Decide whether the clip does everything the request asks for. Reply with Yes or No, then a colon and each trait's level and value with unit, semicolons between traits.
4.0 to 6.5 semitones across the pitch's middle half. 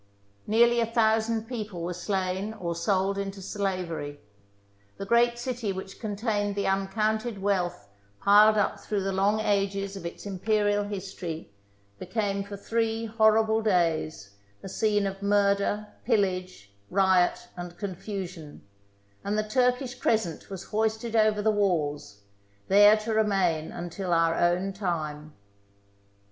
No: average, 2.9 semitones